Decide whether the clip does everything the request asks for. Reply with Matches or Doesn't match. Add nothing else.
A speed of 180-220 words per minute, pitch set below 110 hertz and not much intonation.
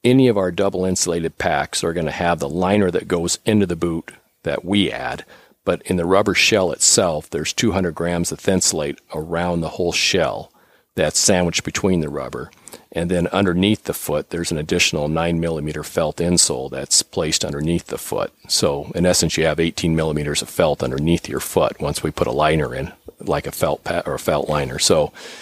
Matches